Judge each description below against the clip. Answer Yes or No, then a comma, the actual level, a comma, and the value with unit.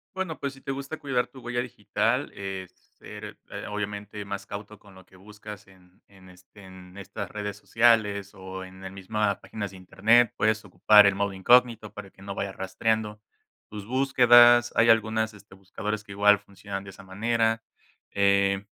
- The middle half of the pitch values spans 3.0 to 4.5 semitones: No, narrow, 2.5 semitones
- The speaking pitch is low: Yes, low, 105 Hz